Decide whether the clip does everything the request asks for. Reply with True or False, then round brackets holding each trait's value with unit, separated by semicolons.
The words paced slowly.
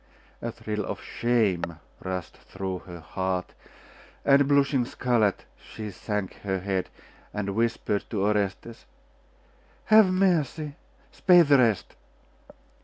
True (110 wpm)